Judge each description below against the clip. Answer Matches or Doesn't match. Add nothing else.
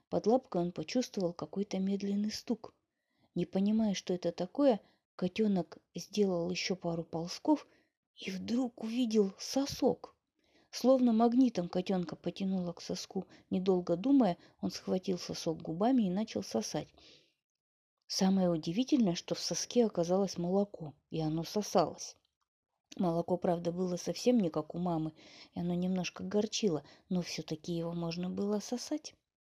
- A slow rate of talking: Doesn't match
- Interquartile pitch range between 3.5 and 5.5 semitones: Matches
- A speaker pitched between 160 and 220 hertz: Matches